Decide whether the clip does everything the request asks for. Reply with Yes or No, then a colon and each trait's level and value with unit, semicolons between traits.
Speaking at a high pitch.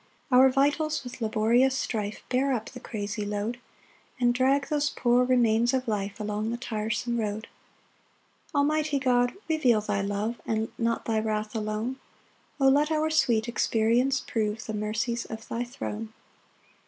Yes: high, 235 Hz